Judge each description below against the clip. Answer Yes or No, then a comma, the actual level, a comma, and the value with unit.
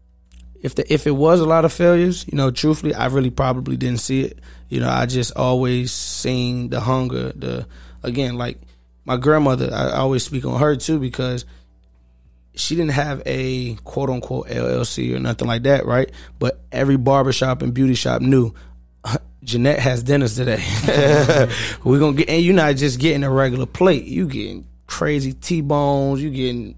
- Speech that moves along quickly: No, average, 175 wpm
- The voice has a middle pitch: No, low, 130 Hz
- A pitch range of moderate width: No, wide, 5.7 semitones